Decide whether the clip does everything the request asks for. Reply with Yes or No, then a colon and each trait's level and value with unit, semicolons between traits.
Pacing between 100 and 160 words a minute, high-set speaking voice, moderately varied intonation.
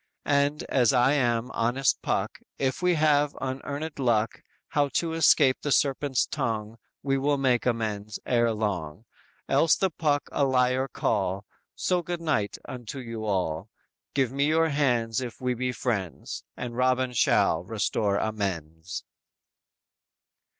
No: average, 140 wpm; low, 125 Hz; average, 4.5 semitones